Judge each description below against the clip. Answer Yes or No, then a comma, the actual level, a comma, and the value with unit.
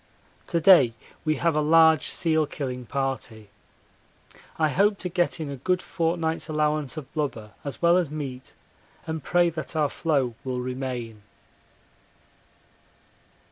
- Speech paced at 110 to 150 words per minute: Yes, average, 140 wpm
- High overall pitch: No, medium, 150 Hz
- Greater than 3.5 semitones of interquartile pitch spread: Yes, average, 4.0 semitones